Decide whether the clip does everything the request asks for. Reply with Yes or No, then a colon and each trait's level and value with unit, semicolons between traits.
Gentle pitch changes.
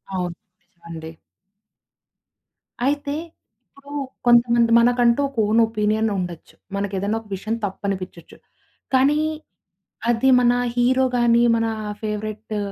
No: average, 3.3 semitones